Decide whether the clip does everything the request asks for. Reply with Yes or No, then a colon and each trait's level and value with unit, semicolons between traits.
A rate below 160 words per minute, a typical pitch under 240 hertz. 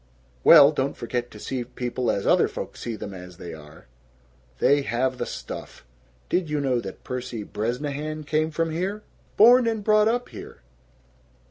No: average, 165 wpm; low, 135 Hz